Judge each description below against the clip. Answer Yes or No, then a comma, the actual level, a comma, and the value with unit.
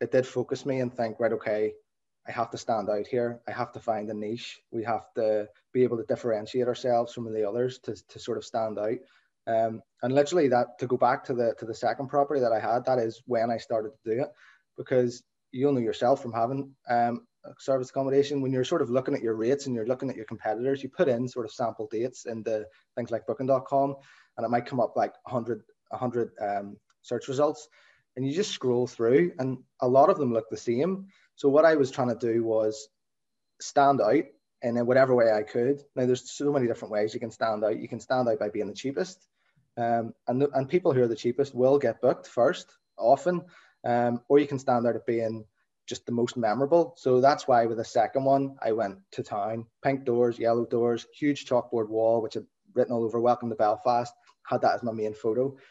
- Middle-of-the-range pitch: No, low, 120 Hz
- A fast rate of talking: Yes, fast, 230 wpm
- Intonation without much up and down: No, average, 3.0 semitones